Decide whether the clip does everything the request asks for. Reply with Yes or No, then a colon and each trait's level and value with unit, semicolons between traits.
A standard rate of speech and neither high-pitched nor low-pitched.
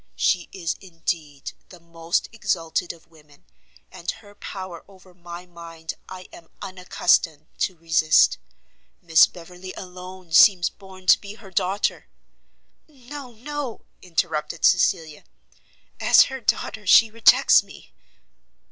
No: slow, 125 wpm; medium, 180 Hz